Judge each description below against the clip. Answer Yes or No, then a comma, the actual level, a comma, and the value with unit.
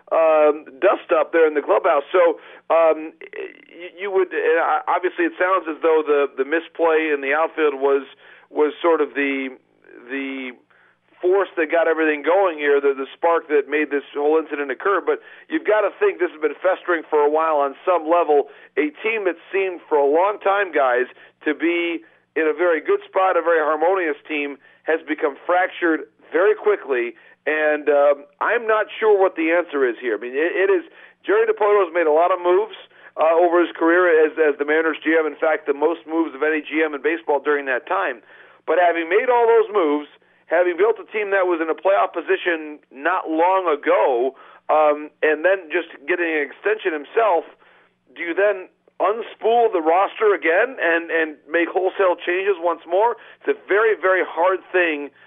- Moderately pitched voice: Yes, medium, 175 Hz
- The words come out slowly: No, average, 190 wpm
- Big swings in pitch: Yes, wide, 6.3 semitones